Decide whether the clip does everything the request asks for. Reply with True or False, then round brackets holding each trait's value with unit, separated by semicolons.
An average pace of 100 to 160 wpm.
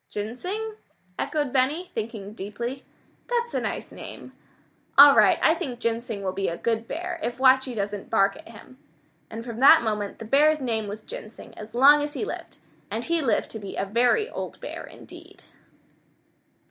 False (180 wpm)